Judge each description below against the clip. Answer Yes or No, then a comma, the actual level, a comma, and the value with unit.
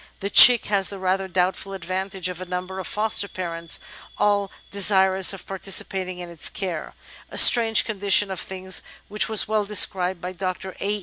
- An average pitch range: No, narrow, 1.7 semitones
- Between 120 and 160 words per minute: No, average, 180 wpm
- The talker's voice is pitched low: No, high, 190 Hz